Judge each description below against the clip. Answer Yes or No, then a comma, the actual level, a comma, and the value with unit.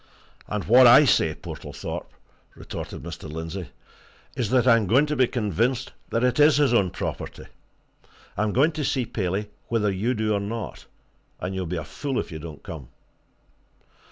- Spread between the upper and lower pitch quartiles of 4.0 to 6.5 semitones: Yes, wide, 5.5 semitones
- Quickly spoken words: No, average, 170 wpm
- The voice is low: Yes, low, 110 Hz